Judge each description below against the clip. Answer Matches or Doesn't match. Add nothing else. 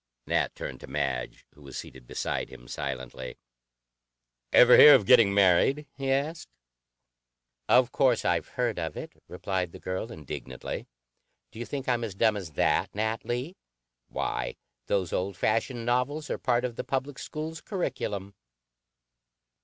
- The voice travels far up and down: Matches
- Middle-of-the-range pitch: Doesn't match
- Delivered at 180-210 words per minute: Doesn't match